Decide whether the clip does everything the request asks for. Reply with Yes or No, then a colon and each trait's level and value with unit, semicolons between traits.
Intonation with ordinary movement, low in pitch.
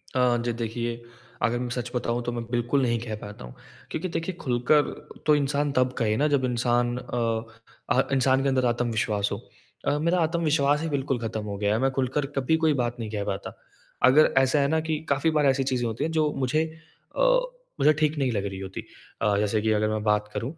Yes: average, 4.1 semitones; low, 125 Hz